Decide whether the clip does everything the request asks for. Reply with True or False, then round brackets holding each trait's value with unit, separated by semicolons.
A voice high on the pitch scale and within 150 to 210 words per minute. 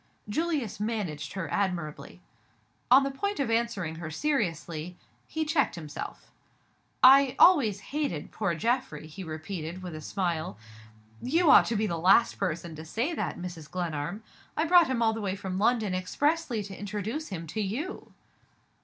True (205 Hz; 160 wpm)